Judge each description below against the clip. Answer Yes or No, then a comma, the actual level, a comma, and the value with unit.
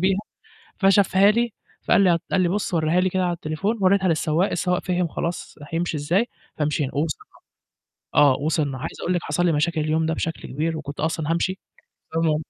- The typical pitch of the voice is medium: Yes, medium, 165 Hz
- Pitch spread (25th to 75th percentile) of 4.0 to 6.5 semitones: No, average, 3.2 semitones